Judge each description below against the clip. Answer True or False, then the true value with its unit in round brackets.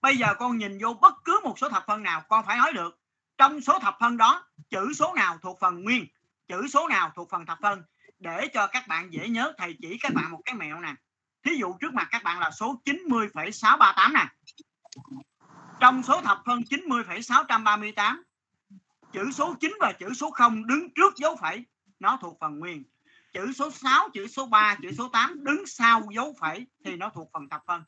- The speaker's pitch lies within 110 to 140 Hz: False (230 Hz)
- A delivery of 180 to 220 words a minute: True (210 wpm)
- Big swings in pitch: True (5.7 semitones)